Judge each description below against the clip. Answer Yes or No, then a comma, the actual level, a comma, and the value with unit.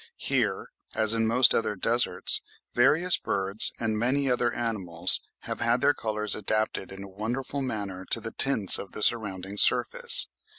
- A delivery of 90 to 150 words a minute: No, average, 160 wpm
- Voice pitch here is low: Yes, low, 110 Hz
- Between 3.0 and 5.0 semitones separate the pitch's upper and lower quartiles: Yes, average, 3.5 semitones